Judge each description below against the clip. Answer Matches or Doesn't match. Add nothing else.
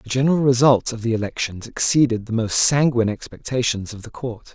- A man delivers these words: Matches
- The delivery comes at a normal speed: Matches